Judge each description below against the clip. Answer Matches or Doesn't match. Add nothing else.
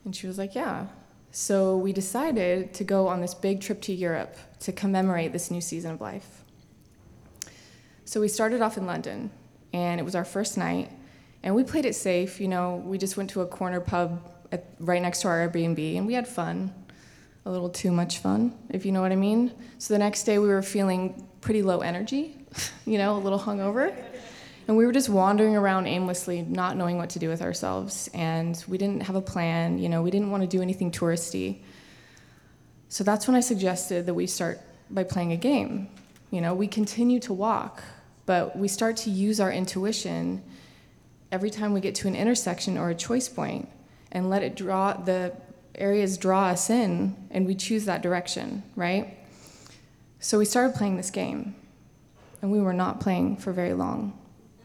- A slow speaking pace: Doesn't match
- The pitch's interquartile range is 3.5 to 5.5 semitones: Doesn't match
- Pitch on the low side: Doesn't match